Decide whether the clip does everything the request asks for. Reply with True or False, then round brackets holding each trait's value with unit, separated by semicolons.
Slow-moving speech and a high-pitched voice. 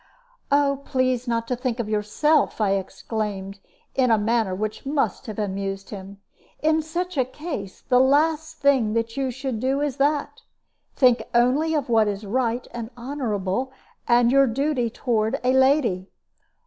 False (160 wpm; 245 Hz)